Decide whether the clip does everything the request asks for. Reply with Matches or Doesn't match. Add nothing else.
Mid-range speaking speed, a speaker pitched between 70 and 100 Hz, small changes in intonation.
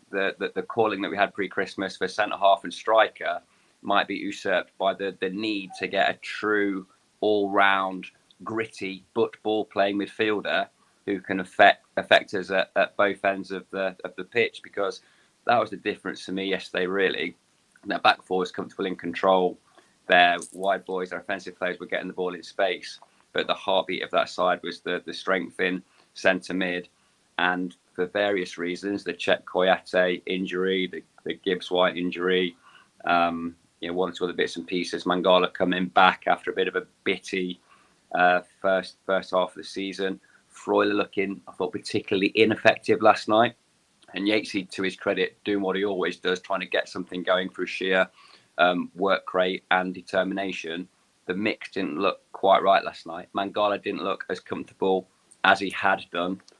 Matches